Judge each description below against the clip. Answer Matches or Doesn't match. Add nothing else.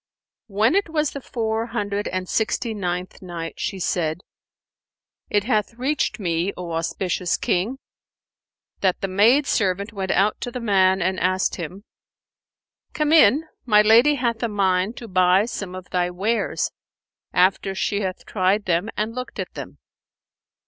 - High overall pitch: Matches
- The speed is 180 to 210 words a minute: Doesn't match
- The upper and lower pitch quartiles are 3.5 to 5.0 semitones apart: Matches